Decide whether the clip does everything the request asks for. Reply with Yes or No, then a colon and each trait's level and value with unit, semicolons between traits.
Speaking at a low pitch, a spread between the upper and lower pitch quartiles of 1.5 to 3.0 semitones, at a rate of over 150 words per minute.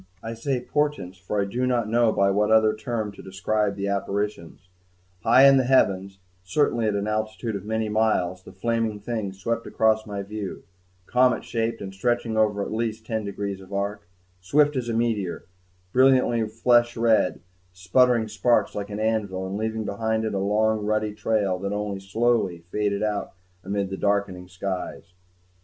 Yes: low, 110 Hz; narrow, 2.5 semitones; average, 175 wpm